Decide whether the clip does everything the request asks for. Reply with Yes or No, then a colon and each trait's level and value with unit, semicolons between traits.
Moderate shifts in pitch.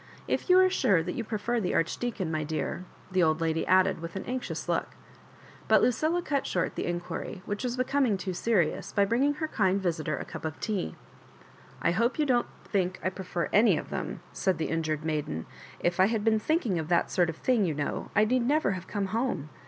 No: wide, 6.1 semitones